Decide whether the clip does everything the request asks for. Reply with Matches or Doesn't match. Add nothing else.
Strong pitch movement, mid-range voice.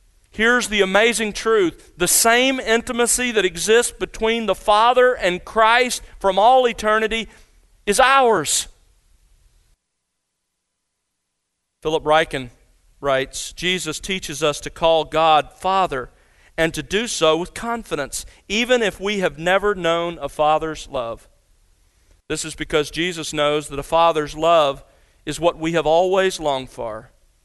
Matches